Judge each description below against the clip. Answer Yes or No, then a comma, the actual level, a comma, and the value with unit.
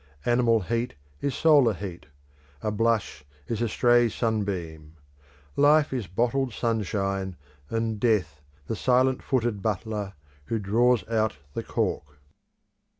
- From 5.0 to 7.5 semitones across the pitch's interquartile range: No, average, 3.6 semitones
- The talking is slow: Yes, slow, 120 wpm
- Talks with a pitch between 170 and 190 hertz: No, low, 110 Hz